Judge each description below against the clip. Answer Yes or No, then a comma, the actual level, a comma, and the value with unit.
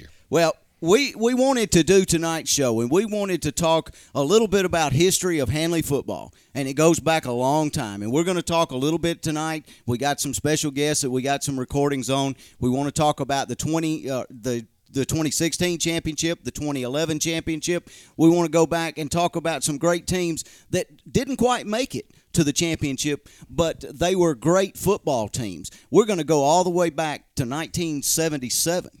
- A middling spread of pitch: Yes, average, 3.3 semitones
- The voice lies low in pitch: No, medium, 160 Hz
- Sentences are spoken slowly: No, fast, 205 wpm